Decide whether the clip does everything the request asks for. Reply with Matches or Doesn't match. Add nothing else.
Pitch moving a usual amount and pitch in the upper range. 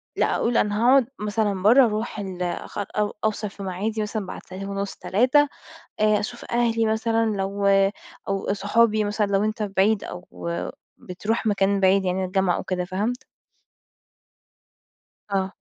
Doesn't match